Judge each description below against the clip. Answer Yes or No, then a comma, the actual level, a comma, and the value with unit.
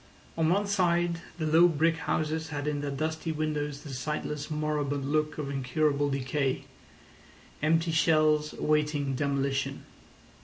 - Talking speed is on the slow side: Yes, slow, 125 wpm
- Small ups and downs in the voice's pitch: Yes, narrow, 2.0 semitones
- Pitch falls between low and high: Yes, medium, 150 Hz